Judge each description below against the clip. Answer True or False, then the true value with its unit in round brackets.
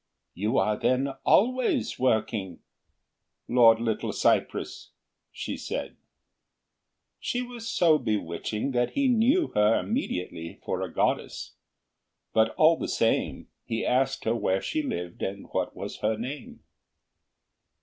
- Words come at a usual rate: False (125 wpm)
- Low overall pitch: True (120 Hz)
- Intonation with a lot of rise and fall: True (9.0 semitones)